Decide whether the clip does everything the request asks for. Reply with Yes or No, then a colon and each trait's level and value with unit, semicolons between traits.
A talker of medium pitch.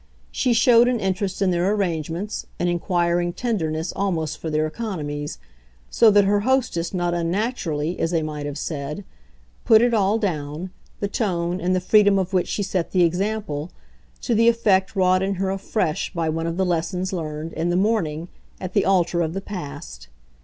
Yes: medium, 180 Hz